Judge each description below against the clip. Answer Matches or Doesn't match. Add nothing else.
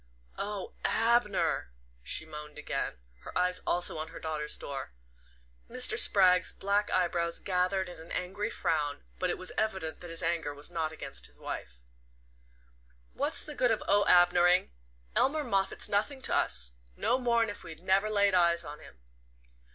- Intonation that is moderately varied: Matches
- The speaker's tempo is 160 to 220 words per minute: Matches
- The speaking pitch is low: Doesn't match